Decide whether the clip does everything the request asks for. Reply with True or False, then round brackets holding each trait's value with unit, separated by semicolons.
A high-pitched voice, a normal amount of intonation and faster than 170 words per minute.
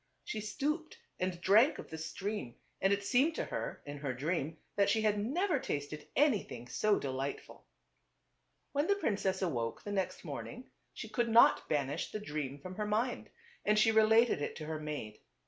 False (200 Hz; 7.0 semitones; 180 wpm)